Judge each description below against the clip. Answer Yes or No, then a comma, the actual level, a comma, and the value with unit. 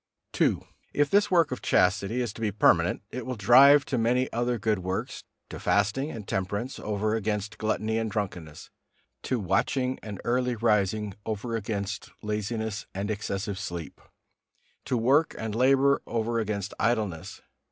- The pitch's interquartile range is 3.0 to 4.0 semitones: Yes, average, 3.4 semitones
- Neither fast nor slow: Yes, average, 150 wpm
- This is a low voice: Yes, low, 110 Hz